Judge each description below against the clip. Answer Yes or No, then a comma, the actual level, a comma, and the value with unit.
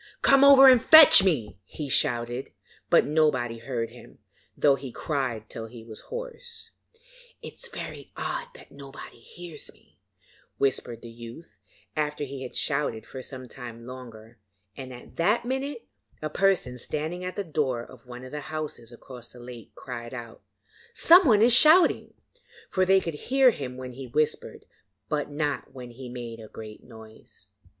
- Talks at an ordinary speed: Yes, average, 165 wpm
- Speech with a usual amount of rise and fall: No, wide, 6.7 semitones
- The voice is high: No, low, 135 Hz